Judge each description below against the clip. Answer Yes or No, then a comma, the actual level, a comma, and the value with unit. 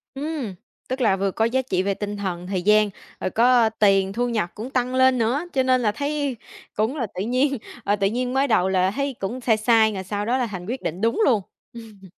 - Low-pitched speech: No, high, 225 Hz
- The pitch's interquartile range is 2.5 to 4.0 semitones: No, average, 4.5 semitones